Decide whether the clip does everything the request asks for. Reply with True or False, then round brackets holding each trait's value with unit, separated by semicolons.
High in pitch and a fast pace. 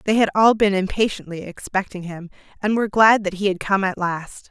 True (195 Hz; 215 wpm)